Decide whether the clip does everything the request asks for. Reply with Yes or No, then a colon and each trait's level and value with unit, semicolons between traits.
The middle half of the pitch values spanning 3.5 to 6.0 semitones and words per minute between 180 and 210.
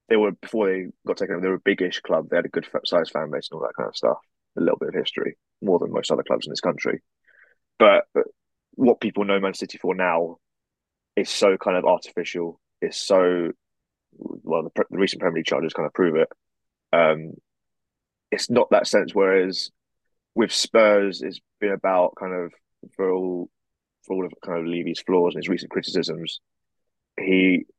No: average, 2.9 semitones; average, 195 wpm